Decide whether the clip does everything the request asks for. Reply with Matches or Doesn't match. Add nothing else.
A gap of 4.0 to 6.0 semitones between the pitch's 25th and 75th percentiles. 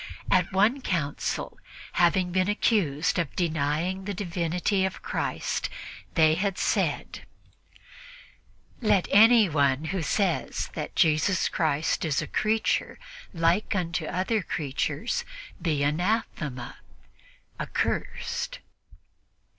Matches